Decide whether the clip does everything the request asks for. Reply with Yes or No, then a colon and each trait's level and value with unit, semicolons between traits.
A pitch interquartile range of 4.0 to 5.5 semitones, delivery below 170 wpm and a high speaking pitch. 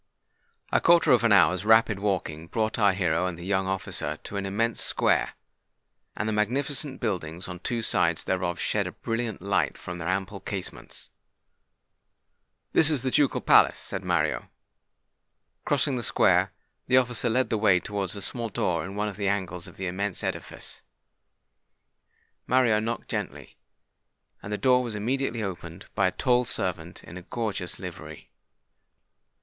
No: average, 4.3 semitones; average, 160 wpm; low, 100 Hz